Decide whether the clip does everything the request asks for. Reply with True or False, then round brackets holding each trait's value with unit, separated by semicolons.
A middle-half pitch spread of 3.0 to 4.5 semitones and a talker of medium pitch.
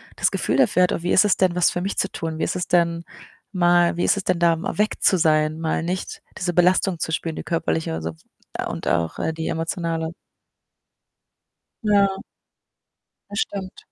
False (2.4 semitones; 175 Hz)